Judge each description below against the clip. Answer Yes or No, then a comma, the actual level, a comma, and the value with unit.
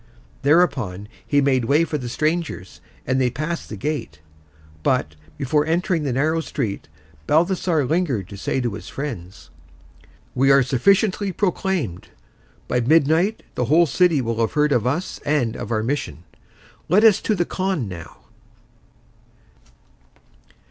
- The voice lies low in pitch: No, medium, 145 Hz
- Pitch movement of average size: No, wide, 5.8 semitones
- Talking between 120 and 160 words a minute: Yes, average, 140 wpm